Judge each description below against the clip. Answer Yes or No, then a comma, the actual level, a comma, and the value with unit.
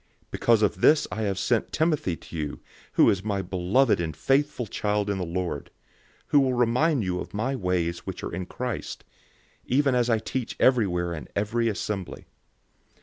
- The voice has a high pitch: No, low, 105 Hz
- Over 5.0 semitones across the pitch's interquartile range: Yes, wide, 5.5 semitones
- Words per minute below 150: No, average, 180 wpm